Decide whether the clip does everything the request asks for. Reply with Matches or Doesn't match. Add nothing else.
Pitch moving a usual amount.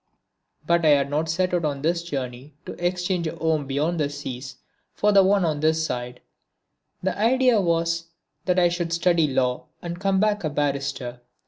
Matches